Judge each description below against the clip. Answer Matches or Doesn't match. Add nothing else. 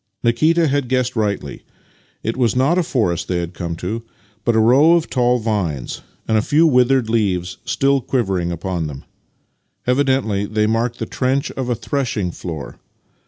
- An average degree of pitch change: Doesn't match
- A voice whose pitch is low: Matches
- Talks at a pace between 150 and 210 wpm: Matches